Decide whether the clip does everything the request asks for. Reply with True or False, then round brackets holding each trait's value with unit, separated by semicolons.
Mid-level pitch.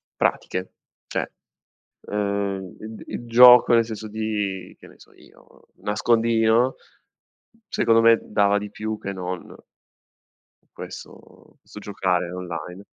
False (105 Hz)